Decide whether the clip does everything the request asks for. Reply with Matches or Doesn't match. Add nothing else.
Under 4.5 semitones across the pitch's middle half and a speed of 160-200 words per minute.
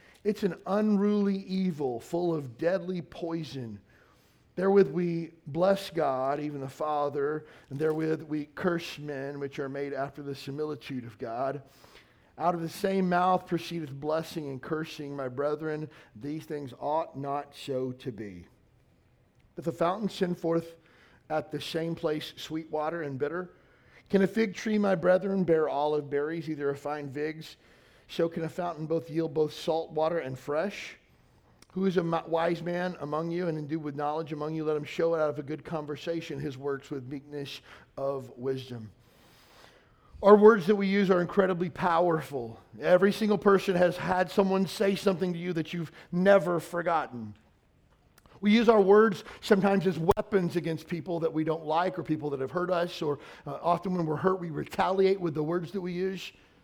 Matches